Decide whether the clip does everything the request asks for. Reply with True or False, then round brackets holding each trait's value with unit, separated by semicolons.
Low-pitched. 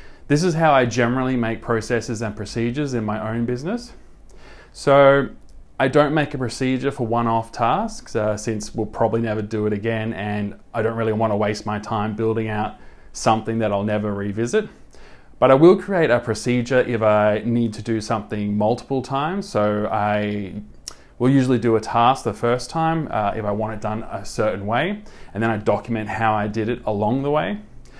True (115 Hz)